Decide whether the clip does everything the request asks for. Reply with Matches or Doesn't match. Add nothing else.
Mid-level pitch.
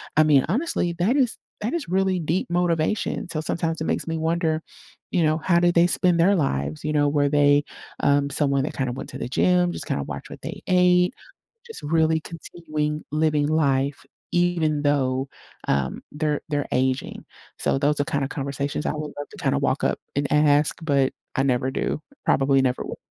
Matches